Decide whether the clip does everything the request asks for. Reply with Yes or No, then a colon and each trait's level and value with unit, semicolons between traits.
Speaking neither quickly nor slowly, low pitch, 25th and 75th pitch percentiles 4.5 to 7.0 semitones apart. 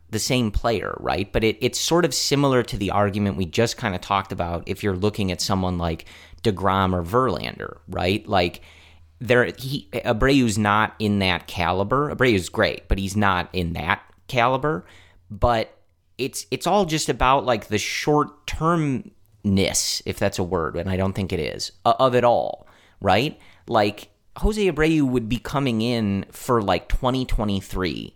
Yes: average, 170 wpm; low, 105 Hz; average, 4.8 semitones